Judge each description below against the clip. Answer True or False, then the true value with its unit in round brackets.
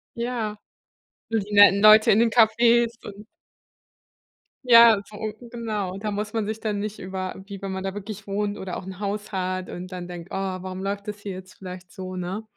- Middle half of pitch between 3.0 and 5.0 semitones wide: False (2.4 semitones)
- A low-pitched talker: False (200 Hz)